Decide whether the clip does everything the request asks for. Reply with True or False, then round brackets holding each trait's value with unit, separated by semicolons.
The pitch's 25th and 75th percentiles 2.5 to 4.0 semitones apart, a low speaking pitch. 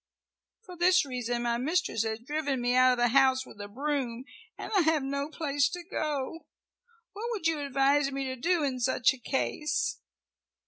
False (3.7 semitones; 275 Hz)